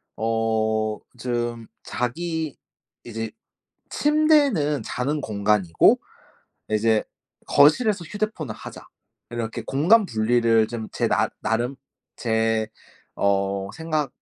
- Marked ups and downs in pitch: Yes, wide, 5.9 semitones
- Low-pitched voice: Yes, low, 120 Hz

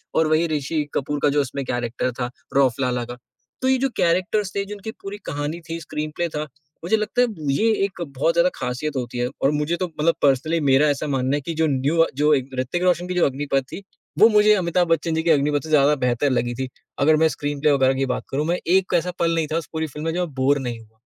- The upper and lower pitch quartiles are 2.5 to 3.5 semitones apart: No, average, 3.9 semitones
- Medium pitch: Yes, medium, 150 Hz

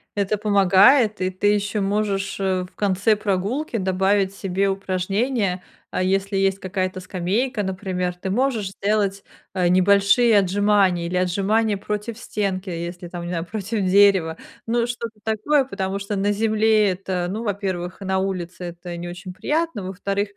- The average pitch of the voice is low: No, high, 195 Hz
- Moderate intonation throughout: No, narrow, 2.2 semitones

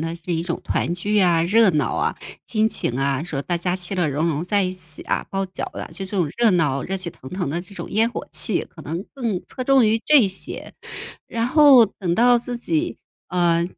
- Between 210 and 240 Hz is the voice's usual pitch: No, medium, 185 Hz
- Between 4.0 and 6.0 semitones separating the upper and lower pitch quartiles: Yes, average, 5.1 semitones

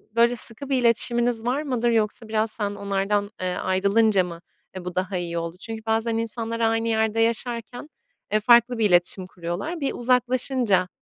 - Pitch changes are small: No, average, 3.1 semitones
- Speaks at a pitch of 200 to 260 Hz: Yes, high, 225 Hz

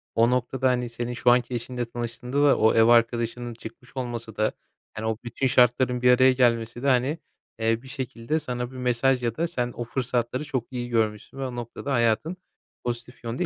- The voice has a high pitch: No, low, 120 Hz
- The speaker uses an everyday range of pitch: No, narrow, 1.6 semitones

